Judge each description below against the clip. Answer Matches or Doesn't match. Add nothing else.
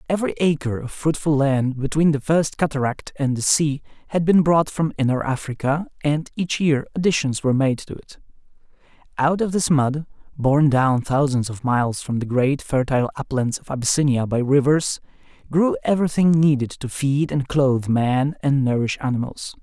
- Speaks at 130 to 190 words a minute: Matches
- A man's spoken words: Matches